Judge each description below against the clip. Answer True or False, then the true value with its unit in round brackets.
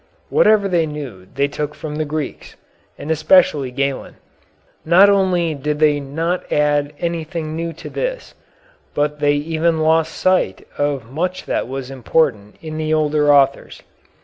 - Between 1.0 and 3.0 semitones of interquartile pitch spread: True (2.5 semitones)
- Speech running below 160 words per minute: True (150 wpm)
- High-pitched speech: False (155 Hz)